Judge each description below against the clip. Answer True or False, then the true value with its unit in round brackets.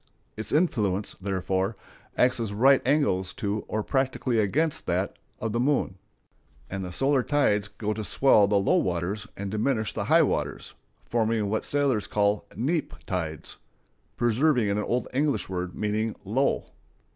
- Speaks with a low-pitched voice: True (110 Hz)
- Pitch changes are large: False (4.7 semitones)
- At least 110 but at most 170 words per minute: True (145 wpm)